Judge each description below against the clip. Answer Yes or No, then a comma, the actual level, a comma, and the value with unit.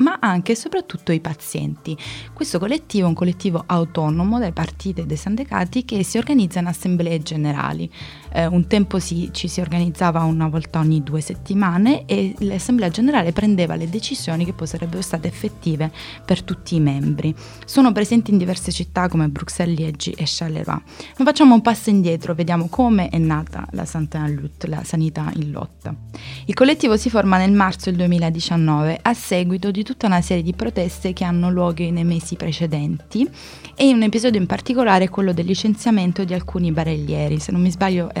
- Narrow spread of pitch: No, average, 3.8 semitones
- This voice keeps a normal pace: No, fast, 180 wpm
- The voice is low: No, medium, 175 Hz